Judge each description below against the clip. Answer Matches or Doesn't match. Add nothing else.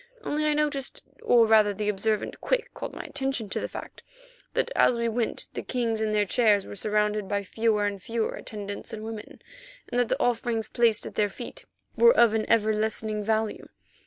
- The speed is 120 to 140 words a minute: Doesn't match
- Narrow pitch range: Matches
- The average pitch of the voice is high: Matches